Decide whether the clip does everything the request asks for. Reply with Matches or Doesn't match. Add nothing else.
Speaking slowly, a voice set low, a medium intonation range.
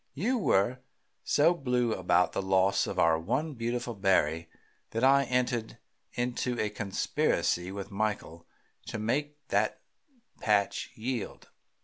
Matches